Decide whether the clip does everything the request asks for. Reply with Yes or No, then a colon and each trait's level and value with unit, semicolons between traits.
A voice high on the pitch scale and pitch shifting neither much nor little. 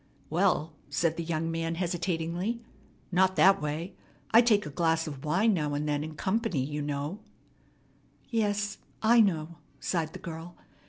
No: medium, 170 Hz; average, 4.0 semitones